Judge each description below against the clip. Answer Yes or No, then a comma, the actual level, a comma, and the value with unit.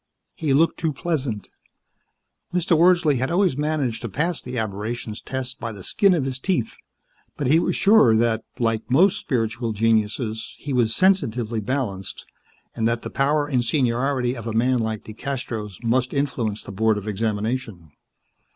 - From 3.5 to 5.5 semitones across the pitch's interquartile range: Yes, average, 4.2 semitones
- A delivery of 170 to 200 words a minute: No, average, 160 wpm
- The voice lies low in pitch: Yes, low, 125 Hz